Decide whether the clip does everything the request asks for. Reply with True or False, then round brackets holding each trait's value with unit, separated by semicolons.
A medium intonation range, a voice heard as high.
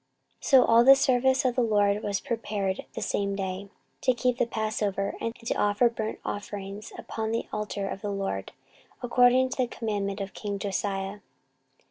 True (3.3 semitones; 210 Hz)